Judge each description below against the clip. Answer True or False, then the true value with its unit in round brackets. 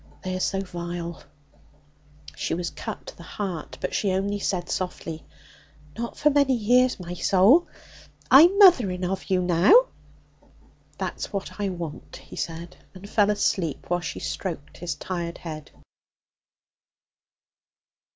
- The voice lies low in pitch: False (185 Hz)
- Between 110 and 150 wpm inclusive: True (135 wpm)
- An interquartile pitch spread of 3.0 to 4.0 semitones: True (3.3 semitones)